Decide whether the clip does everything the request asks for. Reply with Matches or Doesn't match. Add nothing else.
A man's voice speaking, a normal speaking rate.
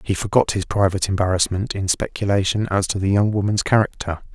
Matches